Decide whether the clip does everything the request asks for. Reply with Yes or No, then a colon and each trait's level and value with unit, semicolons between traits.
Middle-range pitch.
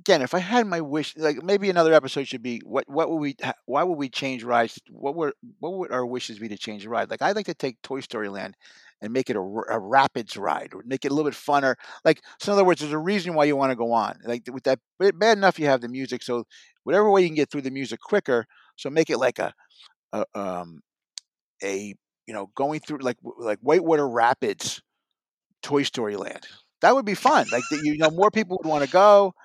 Yes: medium, 145 Hz